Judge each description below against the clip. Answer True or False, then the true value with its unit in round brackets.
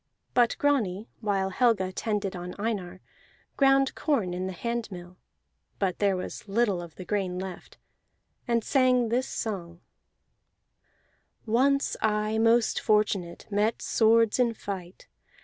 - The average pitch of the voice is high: True (210 Hz)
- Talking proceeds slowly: True (125 wpm)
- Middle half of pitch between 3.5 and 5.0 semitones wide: True (3.9 semitones)